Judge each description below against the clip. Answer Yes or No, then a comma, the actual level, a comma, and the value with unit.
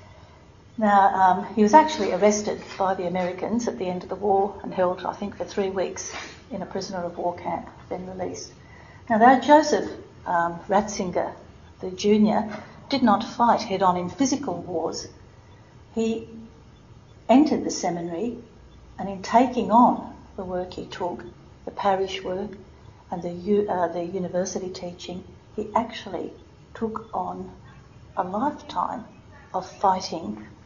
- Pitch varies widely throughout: No, average, 3.6 semitones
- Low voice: No, high, 195 Hz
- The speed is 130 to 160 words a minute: Yes, average, 145 wpm